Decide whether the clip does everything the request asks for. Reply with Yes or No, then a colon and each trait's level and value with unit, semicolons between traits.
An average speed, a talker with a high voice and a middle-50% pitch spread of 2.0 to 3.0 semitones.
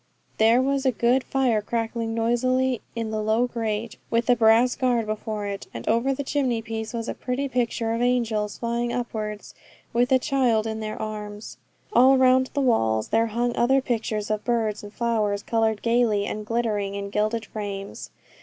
Yes: average, 180 wpm; high, 230 Hz; narrow, 2.4 semitones